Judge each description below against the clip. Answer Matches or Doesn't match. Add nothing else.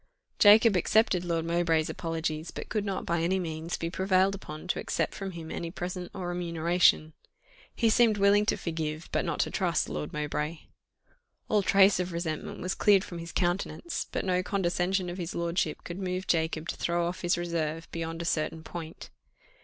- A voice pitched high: Doesn't match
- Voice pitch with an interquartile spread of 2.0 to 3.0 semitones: Matches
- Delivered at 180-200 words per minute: Matches